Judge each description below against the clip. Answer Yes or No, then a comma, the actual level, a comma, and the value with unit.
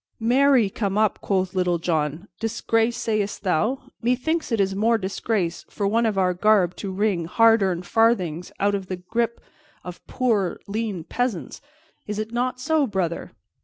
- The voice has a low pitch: No, high, 205 Hz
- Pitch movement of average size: Yes, average, 3.9 semitones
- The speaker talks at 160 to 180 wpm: Yes, average, 165 wpm